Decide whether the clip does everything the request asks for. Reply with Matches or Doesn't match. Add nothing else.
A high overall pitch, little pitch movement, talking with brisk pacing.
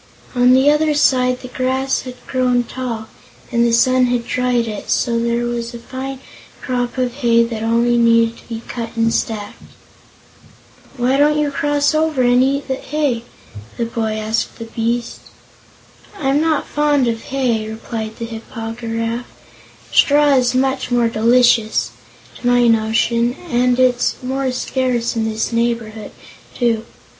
Doesn't match